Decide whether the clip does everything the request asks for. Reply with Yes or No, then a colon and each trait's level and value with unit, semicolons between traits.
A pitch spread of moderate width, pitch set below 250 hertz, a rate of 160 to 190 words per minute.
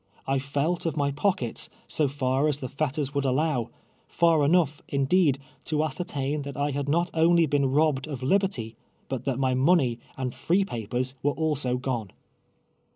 Yes: average, 3.1 semitones; medium, 140 Hz; average, 170 wpm